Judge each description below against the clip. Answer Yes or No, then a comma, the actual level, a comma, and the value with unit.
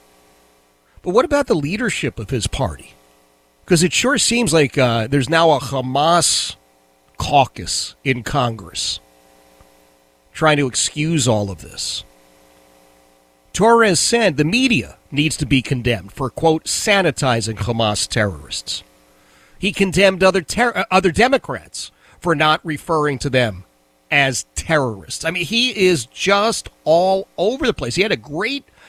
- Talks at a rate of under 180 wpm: Yes, slow, 135 wpm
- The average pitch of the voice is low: Yes, low, 130 Hz